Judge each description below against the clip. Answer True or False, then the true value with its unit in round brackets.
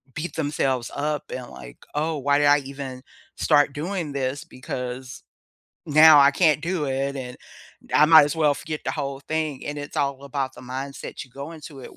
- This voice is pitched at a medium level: True (145 Hz)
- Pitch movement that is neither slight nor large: False (2.3 semitones)